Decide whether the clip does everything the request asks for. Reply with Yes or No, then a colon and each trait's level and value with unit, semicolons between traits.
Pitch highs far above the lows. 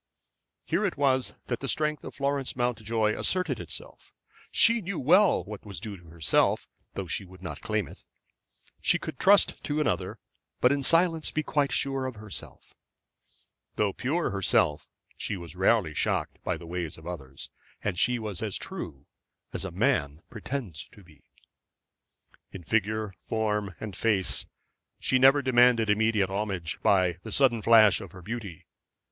Yes: wide, 6.1 semitones